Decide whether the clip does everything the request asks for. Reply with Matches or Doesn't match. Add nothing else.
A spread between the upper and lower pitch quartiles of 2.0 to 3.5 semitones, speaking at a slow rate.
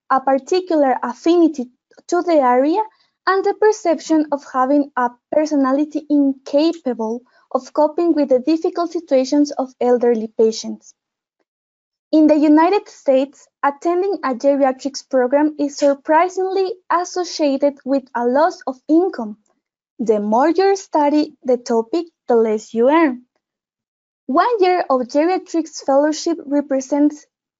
Doesn't match